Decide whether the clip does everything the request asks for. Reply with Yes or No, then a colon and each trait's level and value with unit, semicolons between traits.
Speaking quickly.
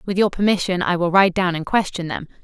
Yes: fast, 245 wpm